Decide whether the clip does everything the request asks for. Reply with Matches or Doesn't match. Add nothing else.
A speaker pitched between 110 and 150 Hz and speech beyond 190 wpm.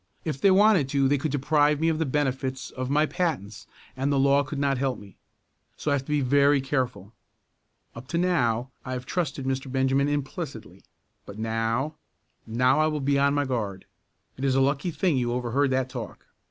Matches